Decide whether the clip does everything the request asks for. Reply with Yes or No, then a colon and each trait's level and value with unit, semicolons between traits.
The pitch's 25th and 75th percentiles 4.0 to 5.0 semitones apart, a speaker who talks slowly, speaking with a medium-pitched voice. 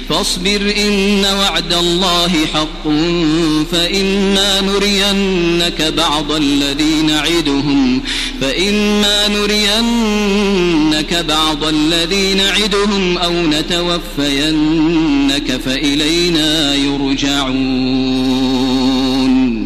Yes: average, 4.5 semitones; slow, 55 wpm; medium, 170 Hz